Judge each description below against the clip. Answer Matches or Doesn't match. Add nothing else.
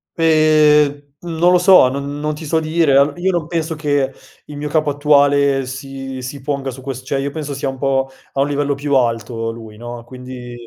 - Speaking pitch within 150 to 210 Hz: Doesn't match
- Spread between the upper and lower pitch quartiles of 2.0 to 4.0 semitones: Matches